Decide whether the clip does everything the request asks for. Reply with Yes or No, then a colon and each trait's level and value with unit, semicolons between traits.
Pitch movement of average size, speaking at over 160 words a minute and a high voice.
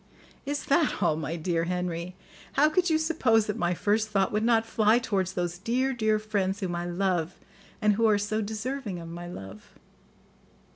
Yes: average, 4.3 semitones; average, 185 wpm; high, 205 Hz